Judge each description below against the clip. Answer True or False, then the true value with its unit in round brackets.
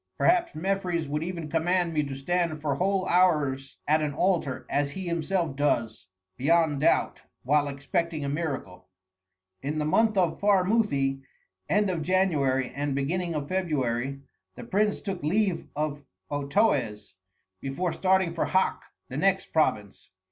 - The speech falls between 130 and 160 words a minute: True (140 wpm)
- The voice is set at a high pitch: False (155 Hz)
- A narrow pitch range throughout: False (4.8 semitones)